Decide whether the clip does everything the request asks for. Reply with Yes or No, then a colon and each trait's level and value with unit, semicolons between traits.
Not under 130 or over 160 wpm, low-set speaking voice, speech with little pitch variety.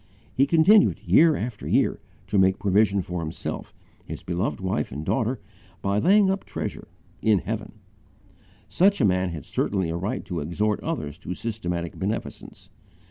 No: average, 155 wpm; low, 100 Hz; average, 5.3 semitones